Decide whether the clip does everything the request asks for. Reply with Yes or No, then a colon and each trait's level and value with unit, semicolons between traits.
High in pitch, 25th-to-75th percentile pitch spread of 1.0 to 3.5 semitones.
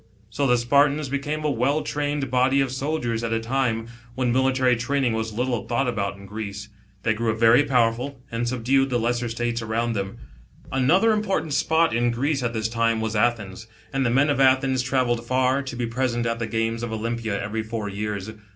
No: low, 120 Hz; average, 2.9 semitones